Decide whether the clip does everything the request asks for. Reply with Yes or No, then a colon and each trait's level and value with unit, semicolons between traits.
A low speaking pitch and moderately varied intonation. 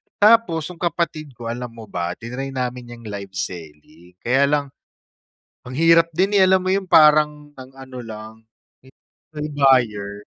No: low, 130 Hz; wide, 5.7 semitones